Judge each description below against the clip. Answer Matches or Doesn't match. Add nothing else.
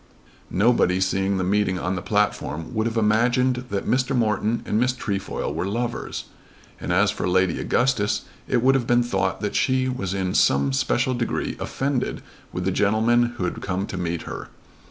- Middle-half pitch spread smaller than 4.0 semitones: Doesn't match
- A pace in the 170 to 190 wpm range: Matches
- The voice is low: Matches